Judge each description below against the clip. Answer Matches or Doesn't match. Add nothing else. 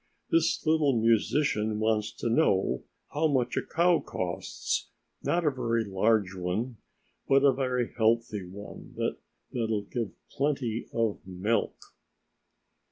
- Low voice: Matches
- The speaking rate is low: Matches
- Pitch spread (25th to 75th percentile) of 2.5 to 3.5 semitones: Doesn't match